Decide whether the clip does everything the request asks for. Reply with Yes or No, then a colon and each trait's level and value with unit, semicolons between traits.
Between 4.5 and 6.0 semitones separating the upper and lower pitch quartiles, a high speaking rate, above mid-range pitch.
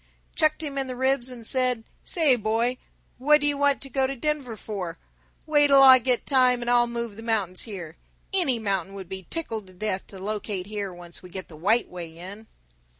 Yes: wide, 5.5 semitones; fast, 210 wpm; high, 235 Hz